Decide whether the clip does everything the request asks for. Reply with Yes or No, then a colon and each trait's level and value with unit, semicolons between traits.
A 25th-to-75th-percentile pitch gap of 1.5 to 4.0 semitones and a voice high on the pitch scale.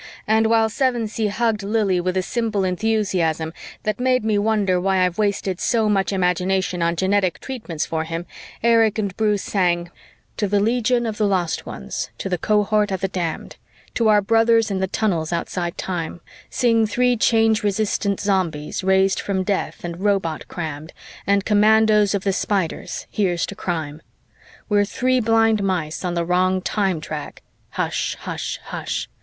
Yes: average, 3.3 semitones; high, 200 Hz